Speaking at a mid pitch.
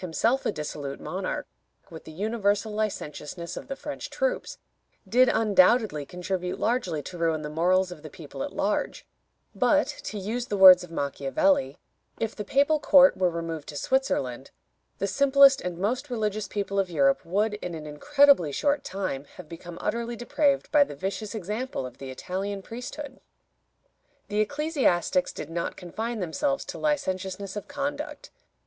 No: high, 200 Hz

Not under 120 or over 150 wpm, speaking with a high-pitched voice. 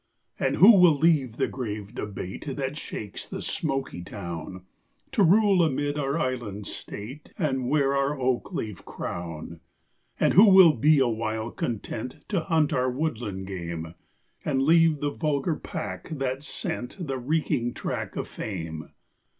No: average, 145 wpm; low, 135 Hz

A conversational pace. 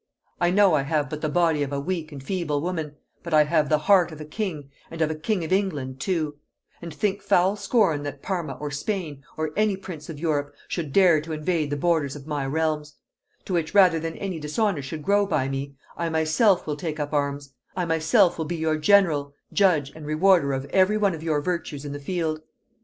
No: fast, 220 wpm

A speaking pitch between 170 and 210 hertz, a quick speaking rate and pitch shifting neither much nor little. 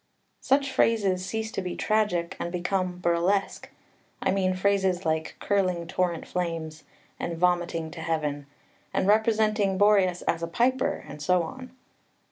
No: medium, 185 Hz; average, 140 wpm; average, 3.2 semitones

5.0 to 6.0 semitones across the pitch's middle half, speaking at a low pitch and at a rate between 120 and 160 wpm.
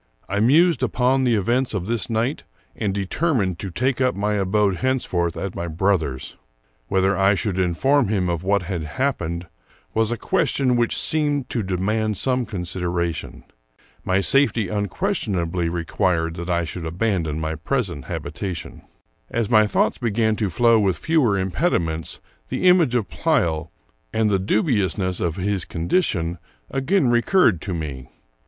Yes: wide, 5.6 semitones; low, 100 Hz; average, 155 wpm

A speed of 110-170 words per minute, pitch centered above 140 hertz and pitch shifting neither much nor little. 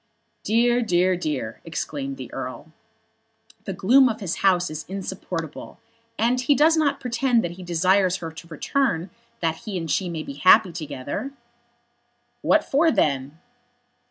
No: average, 150 wpm; high, 190 Hz; wide, 7.1 semitones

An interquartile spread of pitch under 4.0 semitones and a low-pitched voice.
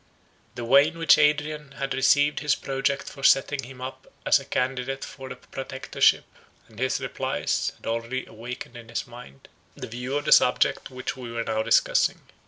Yes: narrow, 2.5 semitones; low, 130 Hz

